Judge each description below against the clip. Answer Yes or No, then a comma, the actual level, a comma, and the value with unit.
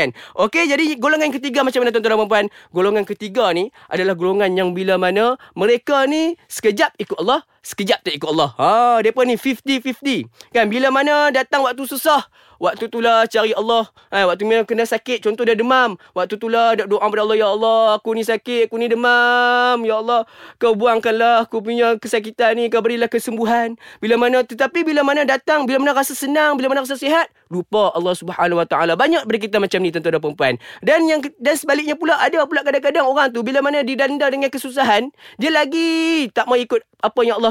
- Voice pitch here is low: No, high, 235 Hz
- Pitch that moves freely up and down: No, average, 3.9 semitones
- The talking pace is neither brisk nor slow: No, fast, 195 wpm